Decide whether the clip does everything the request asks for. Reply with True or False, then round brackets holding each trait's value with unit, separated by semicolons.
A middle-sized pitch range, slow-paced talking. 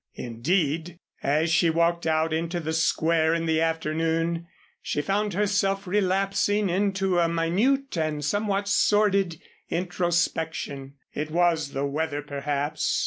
True (3.5 semitones; 125 wpm)